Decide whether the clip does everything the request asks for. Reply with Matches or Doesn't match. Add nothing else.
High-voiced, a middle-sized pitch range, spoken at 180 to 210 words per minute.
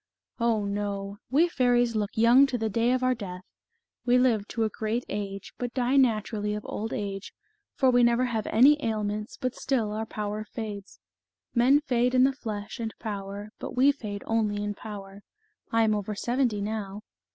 Matches